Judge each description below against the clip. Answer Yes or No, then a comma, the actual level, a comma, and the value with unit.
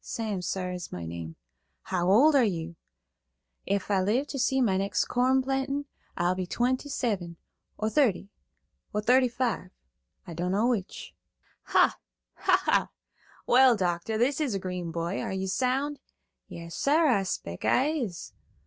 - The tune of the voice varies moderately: No, wide, 6.2 semitones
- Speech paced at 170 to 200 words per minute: No, average, 155 wpm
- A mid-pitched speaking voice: No, high, 210 Hz